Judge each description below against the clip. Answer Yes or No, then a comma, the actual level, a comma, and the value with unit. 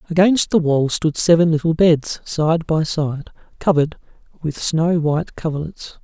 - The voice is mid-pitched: Yes, medium, 160 Hz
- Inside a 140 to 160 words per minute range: Yes, average, 150 wpm